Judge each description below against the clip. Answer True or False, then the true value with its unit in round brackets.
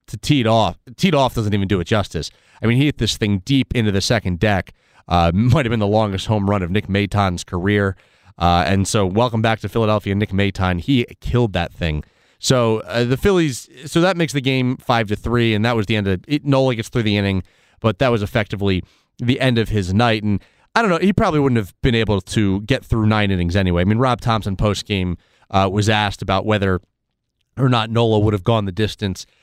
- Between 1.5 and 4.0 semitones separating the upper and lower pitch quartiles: True (3.5 semitones)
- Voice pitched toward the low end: True (110 Hz)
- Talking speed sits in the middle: False (235 wpm)